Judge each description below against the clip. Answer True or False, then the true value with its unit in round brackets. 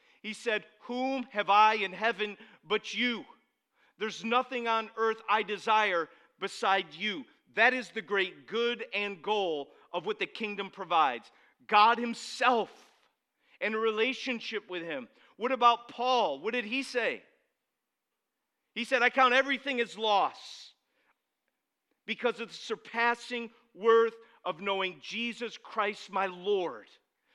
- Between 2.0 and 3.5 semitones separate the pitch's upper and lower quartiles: True (2.9 semitones)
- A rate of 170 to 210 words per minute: False (135 wpm)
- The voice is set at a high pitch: True (225 Hz)